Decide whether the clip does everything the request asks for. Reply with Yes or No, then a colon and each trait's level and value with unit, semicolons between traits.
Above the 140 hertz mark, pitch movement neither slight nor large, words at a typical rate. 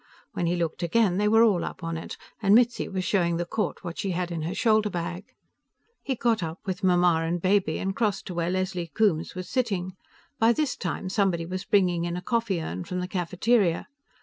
No: medium, 185 Hz; average, 3.3 semitones; fast, 215 wpm